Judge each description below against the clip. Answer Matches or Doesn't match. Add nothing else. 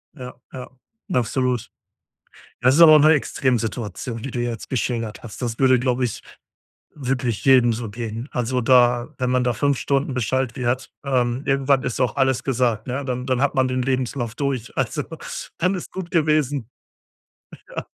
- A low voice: Matches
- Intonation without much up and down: Matches